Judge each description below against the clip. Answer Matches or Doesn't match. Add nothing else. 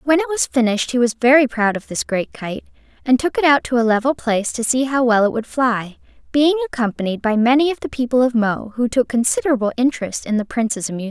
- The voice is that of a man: Doesn't match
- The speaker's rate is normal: Doesn't match